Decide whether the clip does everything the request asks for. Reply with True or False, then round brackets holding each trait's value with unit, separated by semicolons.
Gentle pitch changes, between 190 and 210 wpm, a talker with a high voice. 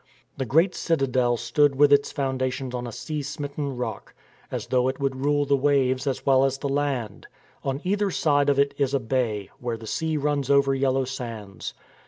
False (2.1 semitones; 195 wpm; 135 Hz)